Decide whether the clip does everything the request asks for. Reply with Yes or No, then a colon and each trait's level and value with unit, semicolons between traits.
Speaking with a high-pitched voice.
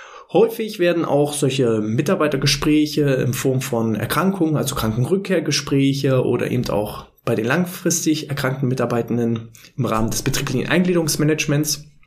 No: medium, 140 Hz